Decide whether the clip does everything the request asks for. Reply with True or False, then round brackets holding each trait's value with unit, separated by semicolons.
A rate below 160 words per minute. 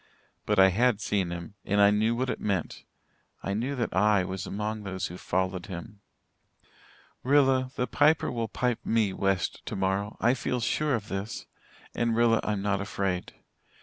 False (170 wpm)